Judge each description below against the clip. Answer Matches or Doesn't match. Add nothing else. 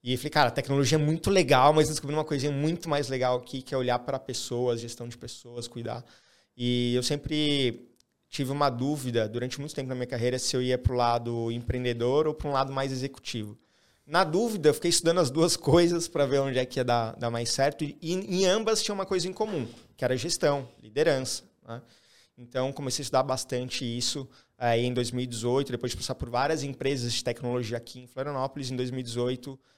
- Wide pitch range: Doesn't match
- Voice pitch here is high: Doesn't match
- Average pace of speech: Doesn't match